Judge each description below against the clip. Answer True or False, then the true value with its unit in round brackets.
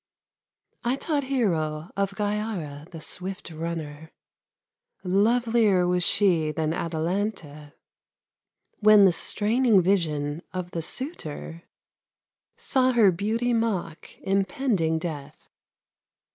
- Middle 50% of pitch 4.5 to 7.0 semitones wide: True (5.2 semitones)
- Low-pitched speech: False (185 Hz)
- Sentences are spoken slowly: True (95 wpm)